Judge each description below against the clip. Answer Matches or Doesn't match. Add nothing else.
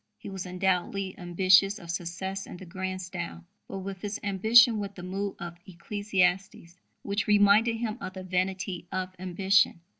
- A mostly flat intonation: Matches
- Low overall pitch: Doesn't match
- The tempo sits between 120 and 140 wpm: Doesn't match